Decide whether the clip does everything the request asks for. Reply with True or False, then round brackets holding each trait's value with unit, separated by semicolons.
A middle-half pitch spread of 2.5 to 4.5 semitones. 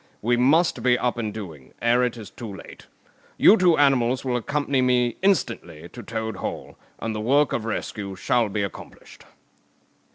True (3.4 semitones)